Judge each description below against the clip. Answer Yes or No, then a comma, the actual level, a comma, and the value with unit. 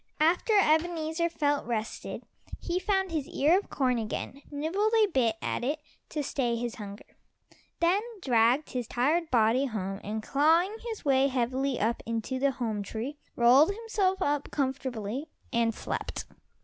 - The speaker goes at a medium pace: Yes, average, 150 wpm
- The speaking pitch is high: Yes, very high, 275 Hz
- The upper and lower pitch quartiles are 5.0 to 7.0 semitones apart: Yes, wide, 5.6 semitones